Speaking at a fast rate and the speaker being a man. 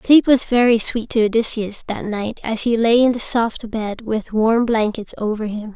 No: fast, 210 wpm; female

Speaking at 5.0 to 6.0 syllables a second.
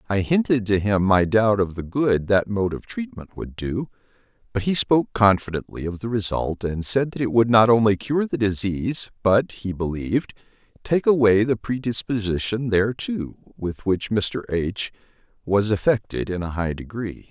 No: 4.8 syllables/s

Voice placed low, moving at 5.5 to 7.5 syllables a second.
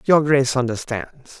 No: low, 130 Hz; 4.7 syllables/s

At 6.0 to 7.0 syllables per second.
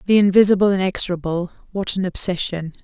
Yes: 6.3 syllables/s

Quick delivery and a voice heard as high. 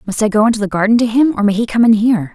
Yes: fast, 360 wpm; high, 220 Hz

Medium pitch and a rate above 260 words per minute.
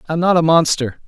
Yes: medium, 160 Hz; fast, 280 wpm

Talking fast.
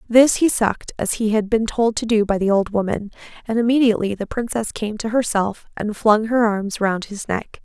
Yes: fast, 220 wpm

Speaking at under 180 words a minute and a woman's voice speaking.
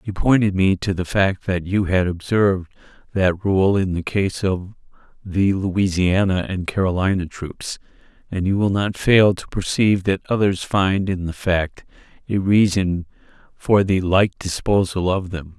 No: average, 160 wpm; male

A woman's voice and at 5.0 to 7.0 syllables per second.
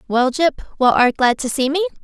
Yes: female; 5.3 syllables/s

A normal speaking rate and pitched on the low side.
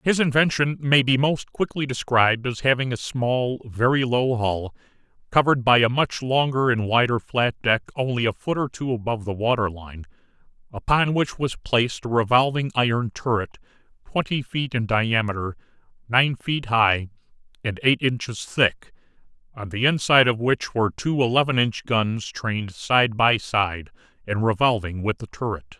Yes: average, 165 wpm; low, 120 Hz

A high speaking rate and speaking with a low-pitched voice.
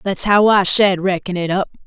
No: fast, 225 wpm; high, 195 Hz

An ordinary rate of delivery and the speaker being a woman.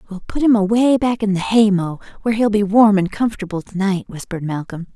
No: fast, 230 wpm; female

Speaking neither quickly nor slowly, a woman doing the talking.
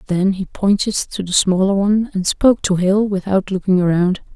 Yes: average, 195 wpm; female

